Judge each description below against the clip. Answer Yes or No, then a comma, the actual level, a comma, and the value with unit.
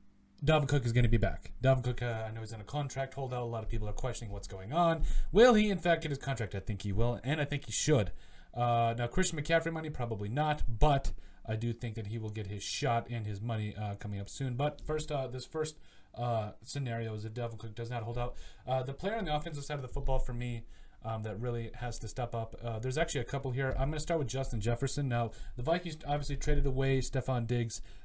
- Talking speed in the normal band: No, fast, 260 wpm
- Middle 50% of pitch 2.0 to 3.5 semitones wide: No, average, 4.2 semitones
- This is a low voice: Yes, low, 120 Hz